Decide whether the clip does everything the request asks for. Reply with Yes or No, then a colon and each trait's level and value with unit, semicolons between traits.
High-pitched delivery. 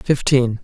No: low, 125 Hz